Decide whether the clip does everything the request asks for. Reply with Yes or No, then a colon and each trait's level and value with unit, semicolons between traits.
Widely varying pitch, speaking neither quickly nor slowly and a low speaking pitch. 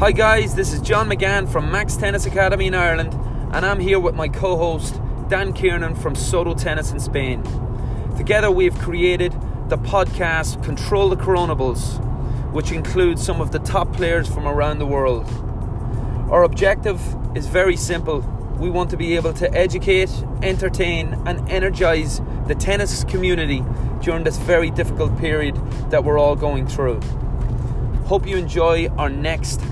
Yes: wide, 5.7 semitones; average, 160 wpm; low, 130 Hz